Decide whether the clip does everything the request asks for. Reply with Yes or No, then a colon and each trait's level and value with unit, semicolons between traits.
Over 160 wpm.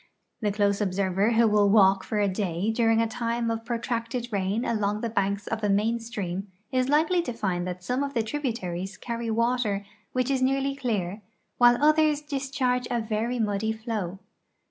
Yes: average, 185 wpm